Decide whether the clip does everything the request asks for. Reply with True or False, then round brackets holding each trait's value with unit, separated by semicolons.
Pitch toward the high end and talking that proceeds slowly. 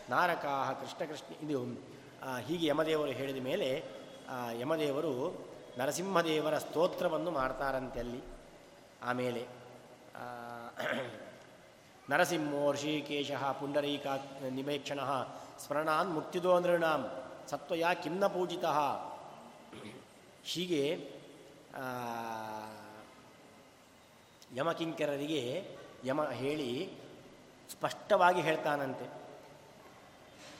False (145 Hz; 60 wpm)